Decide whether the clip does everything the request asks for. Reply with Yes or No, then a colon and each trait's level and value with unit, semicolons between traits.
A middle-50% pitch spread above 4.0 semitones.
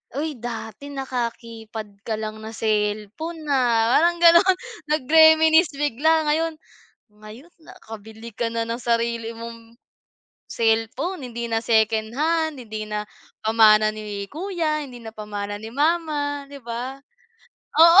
Yes: wide, 5.6 semitones